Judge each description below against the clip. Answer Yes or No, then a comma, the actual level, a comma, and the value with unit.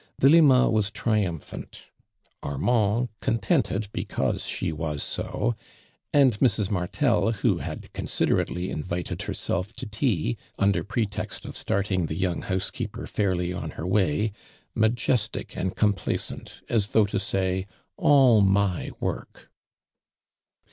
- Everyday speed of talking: No, slow, 125 wpm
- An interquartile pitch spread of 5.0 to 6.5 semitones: No, average, 3.6 semitones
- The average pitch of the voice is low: Yes, low, 100 Hz